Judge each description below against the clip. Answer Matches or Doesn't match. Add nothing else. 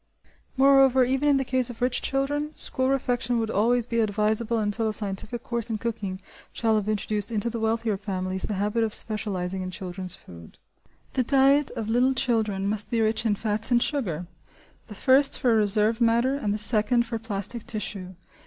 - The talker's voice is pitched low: Doesn't match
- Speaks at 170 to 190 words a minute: Matches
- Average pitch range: Matches